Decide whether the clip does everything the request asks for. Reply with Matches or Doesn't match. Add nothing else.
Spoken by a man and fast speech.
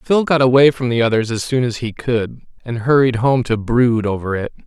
Matches